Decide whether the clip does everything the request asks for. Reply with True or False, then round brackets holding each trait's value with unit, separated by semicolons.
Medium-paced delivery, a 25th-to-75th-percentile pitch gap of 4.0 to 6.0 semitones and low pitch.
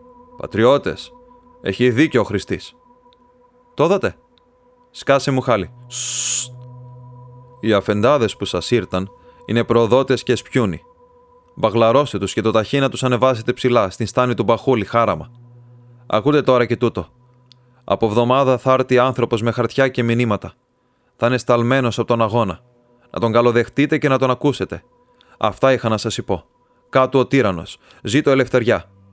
False (140 wpm; 2.5 semitones; 125 Hz)